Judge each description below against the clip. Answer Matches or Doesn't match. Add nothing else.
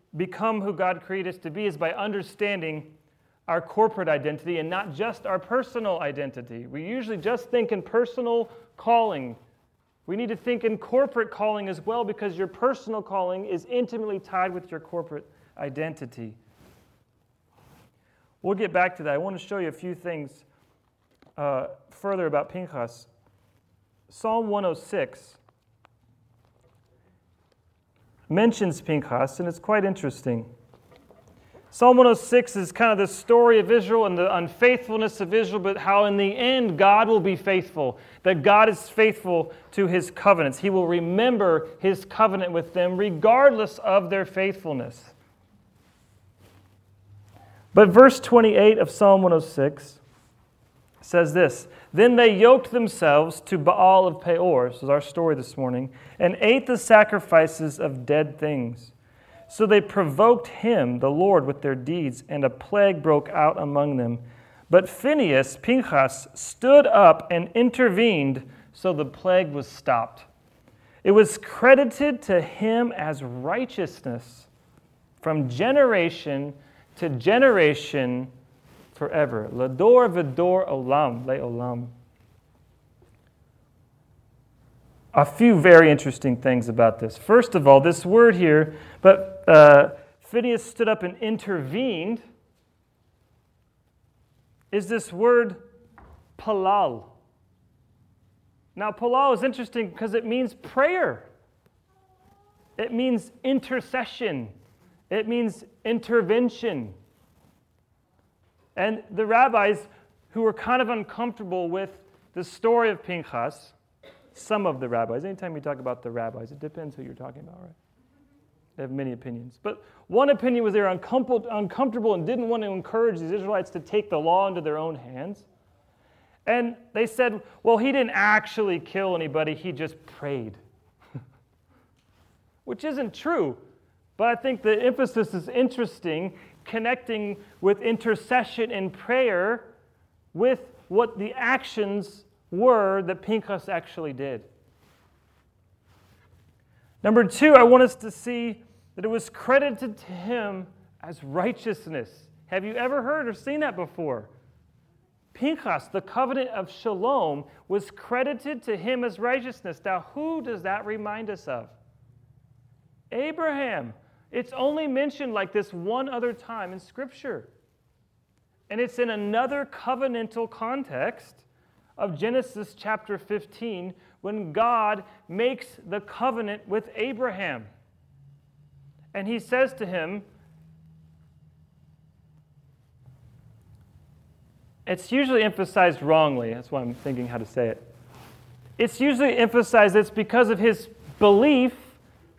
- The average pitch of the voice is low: Doesn't match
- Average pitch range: Doesn't match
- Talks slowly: Matches